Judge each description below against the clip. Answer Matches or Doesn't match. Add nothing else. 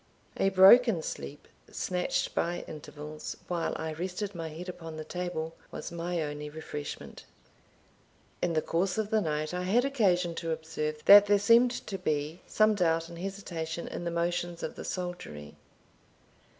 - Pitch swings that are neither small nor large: Matches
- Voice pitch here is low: Doesn't match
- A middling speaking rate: Matches